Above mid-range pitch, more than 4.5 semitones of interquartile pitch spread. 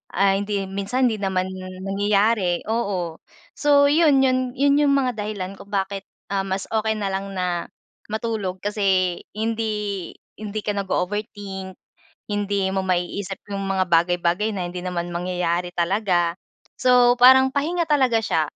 No: high, 200 Hz; average, 3.4 semitones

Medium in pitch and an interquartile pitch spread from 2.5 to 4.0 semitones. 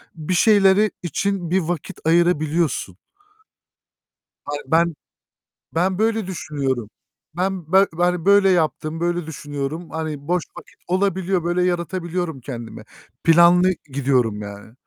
Yes: medium, 170 Hz; average, 3.6 semitones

